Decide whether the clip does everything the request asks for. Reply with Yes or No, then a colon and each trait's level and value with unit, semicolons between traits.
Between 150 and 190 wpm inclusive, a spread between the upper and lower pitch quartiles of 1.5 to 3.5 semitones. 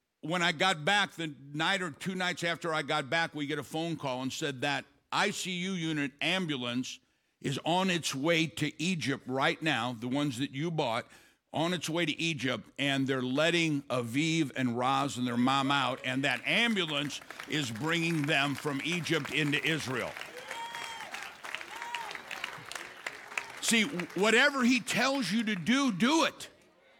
No: average, 160 wpm; average, 4.6 semitones